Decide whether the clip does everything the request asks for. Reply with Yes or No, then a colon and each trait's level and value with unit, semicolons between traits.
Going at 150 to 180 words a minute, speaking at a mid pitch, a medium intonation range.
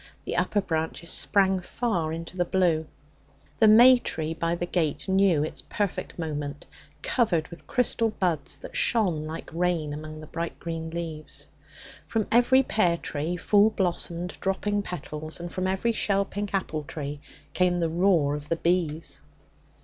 Yes: average, 155 wpm; medium, 175 Hz; average, 3.7 semitones